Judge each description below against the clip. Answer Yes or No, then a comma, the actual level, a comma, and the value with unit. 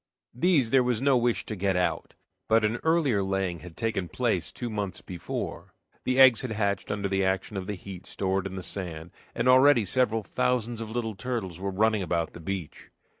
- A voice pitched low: Yes, low, 105 Hz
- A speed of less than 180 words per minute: No, average, 200 wpm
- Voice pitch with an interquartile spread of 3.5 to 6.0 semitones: Yes, average, 4.2 semitones